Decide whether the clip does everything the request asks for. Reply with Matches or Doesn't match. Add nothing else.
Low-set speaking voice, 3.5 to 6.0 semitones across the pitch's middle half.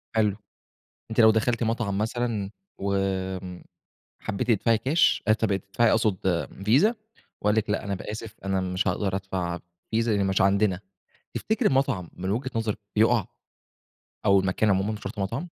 Doesn't match